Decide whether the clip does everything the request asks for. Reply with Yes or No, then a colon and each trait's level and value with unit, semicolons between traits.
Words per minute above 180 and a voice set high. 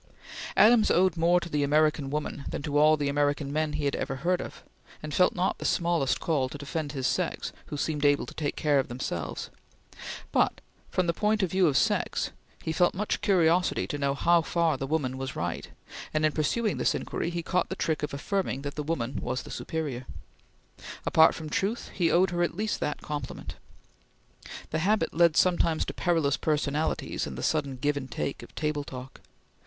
No: average, 200 wpm; medium, 155 Hz